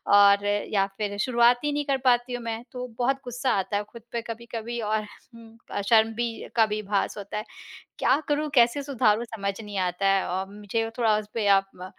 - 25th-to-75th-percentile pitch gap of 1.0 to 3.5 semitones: Yes, average, 2.9 semitones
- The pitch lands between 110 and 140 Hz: No, high, 225 Hz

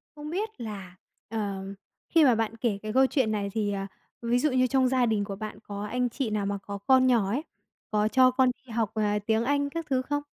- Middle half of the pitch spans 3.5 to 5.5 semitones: Yes, average, 3.9 semitones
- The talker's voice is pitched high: Yes, high, 230 Hz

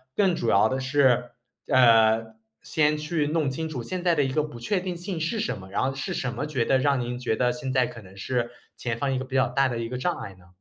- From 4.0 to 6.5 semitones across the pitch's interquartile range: Yes, average, 4.3 semitones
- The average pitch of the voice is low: Yes, low, 130 Hz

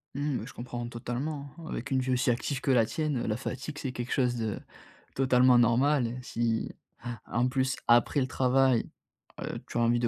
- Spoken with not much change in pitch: Yes, narrow, 2.1 semitones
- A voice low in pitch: Yes, low, 125 Hz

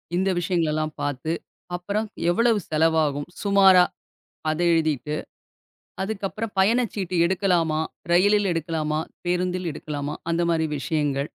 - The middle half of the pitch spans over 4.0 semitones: No, average, 3.7 semitones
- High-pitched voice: No, medium, 170 Hz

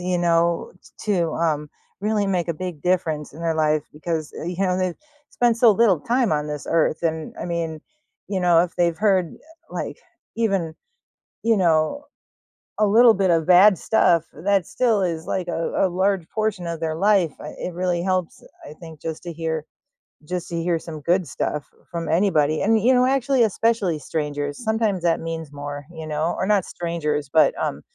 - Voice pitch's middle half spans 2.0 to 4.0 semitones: Yes, average, 3.5 semitones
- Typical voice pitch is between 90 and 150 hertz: No, medium, 170 Hz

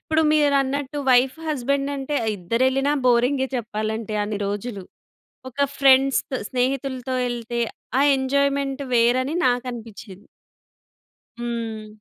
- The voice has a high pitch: Yes, very high, 255 Hz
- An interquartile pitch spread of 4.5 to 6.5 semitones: No, average, 2.9 semitones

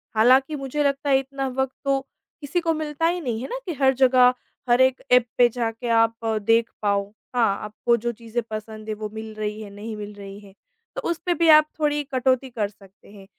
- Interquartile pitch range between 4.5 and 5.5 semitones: No, average, 4.0 semitones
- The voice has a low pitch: No, high, 240 Hz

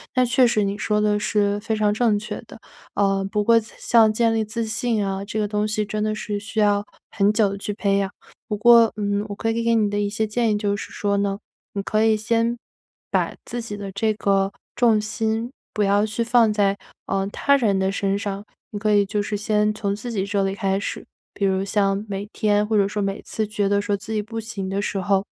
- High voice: Yes, high, 210 Hz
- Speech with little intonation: Yes, narrow, 1.5 semitones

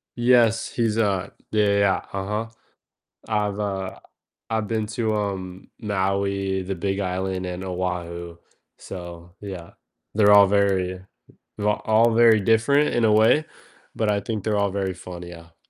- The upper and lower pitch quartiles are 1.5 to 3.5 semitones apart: Yes, average, 2.7 semitones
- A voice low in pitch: Yes, low, 100 Hz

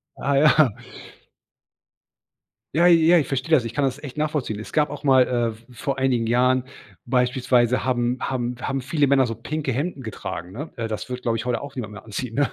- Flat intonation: No, average, 3.0 semitones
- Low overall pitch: Yes, low, 130 Hz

